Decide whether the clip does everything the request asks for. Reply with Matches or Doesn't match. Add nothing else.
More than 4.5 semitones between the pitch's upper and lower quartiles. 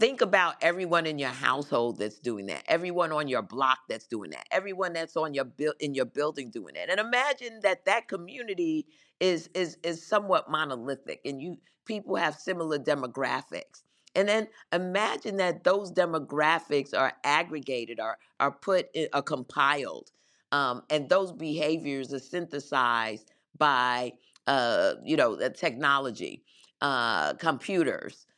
Matches